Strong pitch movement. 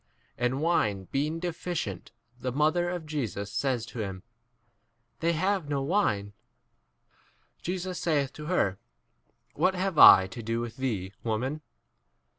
Yes: wide, 7.7 semitones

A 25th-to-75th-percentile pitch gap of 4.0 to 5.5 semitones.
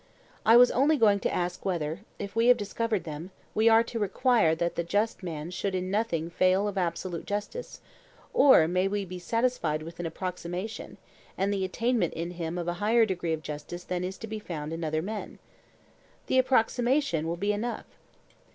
Yes: average, 4.6 semitones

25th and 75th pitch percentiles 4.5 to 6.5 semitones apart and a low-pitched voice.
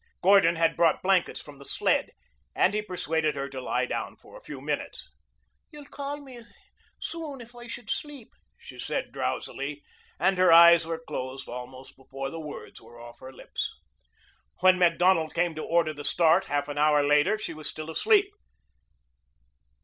No: wide, 5.6 semitones; medium, 165 Hz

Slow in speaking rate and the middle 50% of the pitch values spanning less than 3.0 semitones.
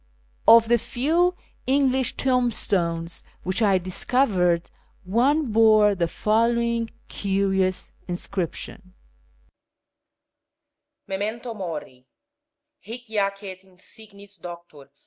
No: slow, 90 wpm; average, 4.2 semitones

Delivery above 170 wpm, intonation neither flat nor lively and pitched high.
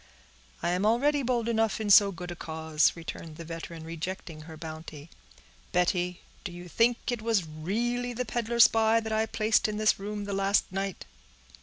Yes: average, 180 wpm; average, 5.0 semitones; high, 195 Hz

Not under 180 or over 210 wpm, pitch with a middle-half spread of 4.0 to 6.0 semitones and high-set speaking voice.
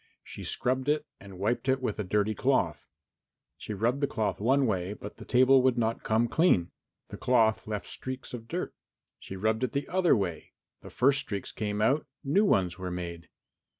No: average, 190 wpm; average, 4.5 semitones; low, 115 Hz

